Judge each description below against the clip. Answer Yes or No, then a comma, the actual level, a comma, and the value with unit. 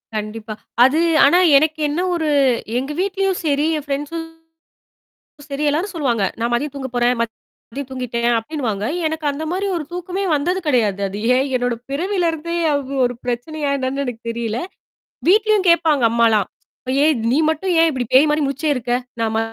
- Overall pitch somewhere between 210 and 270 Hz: No, very high, 280 Hz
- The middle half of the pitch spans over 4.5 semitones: Yes, average, 5.0 semitones